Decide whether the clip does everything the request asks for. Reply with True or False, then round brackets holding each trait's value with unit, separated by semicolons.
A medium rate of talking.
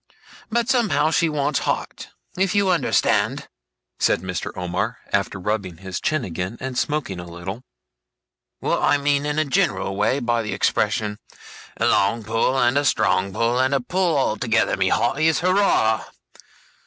True (155 wpm)